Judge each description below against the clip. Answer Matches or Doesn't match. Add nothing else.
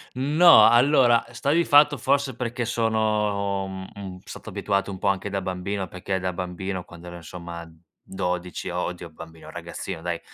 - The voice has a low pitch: Matches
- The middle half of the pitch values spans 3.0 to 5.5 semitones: Matches